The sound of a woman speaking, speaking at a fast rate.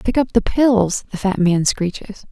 Yes: female; fast, 210 wpm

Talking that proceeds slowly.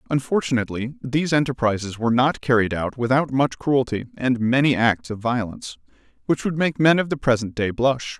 No: average, 175 wpm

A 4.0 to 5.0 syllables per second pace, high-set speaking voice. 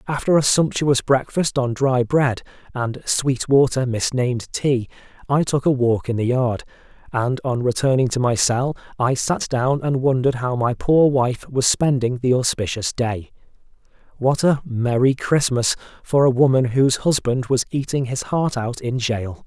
No: 4.5 syllables/s; low, 130 Hz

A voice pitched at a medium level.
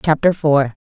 Yes: medium, 160 Hz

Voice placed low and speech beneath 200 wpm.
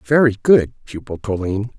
Yes: low, 110 Hz; slow, 135 wpm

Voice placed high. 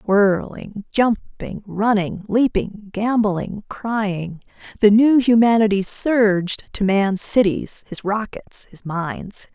Yes: high, 205 Hz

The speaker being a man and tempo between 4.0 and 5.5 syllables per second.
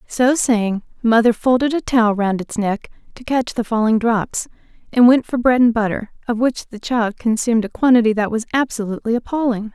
No: female; 5.4 syllables/s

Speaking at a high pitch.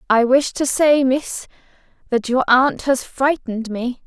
Yes: very high, 260 Hz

